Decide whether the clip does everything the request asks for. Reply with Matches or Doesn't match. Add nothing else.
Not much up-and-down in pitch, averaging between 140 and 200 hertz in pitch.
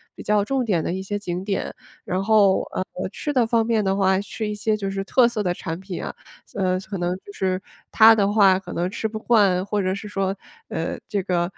Matches